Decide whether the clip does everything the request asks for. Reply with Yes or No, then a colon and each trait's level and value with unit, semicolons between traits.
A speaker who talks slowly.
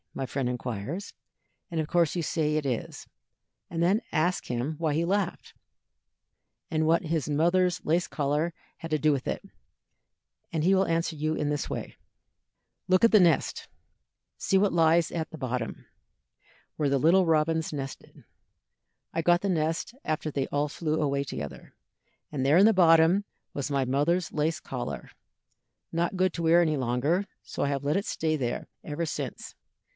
No: average, 170 wpm